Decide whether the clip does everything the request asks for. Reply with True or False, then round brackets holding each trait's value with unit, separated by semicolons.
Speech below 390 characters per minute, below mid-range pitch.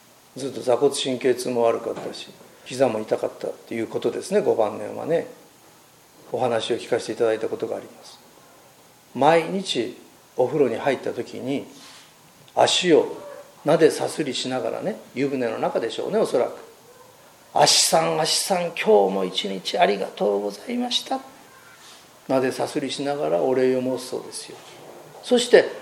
False (305 characters per minute; 165 Hz)